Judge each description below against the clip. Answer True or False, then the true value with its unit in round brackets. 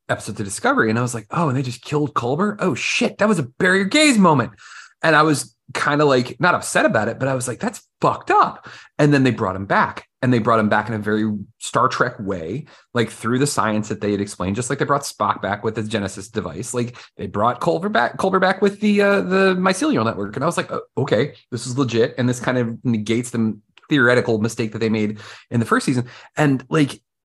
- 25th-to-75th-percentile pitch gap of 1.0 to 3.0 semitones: False (5.2 semitones)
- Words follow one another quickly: True (245 wpm)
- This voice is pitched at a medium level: False (125 Hz)